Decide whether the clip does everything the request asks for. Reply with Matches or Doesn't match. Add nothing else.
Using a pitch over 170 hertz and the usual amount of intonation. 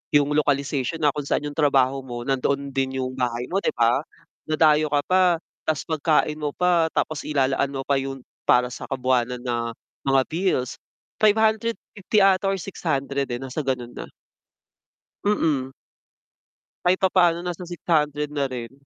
Doesn't match